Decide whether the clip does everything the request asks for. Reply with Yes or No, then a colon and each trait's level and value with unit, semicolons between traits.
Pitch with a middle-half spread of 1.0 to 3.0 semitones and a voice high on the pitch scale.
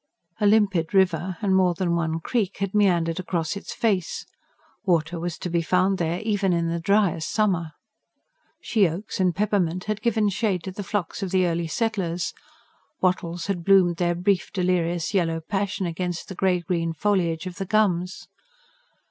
No: average, 2.7 semitones; medium, 180 Hz